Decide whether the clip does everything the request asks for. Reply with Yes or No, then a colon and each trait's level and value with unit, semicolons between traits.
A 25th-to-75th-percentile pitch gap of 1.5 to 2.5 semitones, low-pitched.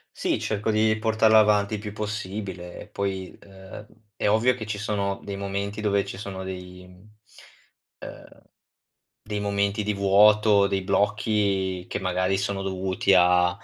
Yes: narrow, 1.8 semitones; low, 100 Hz